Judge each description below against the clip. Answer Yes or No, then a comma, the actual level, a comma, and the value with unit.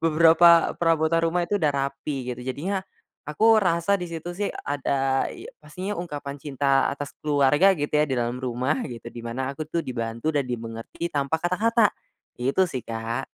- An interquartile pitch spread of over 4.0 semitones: Yes, average, 4.4 semitones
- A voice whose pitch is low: No, medium, 145 Hz